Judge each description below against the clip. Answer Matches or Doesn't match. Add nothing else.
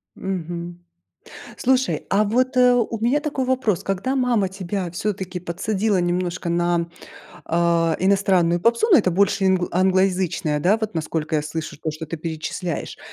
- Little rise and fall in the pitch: Doesn't match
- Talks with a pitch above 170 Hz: Matches